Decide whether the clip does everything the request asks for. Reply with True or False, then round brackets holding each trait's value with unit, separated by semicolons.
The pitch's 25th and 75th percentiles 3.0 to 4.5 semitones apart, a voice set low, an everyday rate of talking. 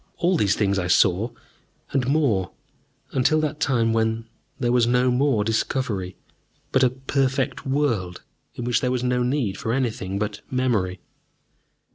True (4.2 semitones; 120 Hz; 150 wpm)